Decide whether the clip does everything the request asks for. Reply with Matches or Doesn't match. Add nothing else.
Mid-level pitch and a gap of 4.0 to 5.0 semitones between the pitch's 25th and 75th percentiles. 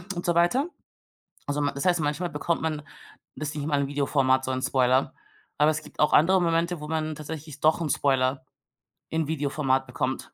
Doesn't match